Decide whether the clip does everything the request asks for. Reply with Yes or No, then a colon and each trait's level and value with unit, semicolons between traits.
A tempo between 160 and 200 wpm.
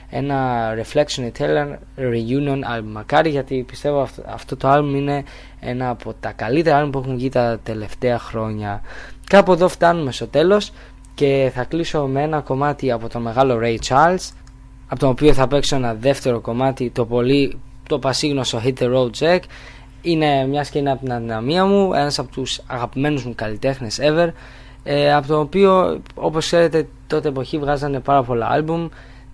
Yes: average, 170 wpm